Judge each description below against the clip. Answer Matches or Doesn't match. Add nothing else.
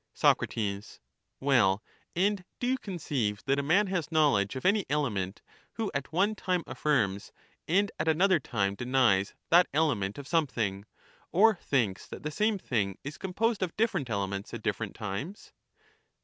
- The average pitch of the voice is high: Doesn't match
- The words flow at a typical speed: Matches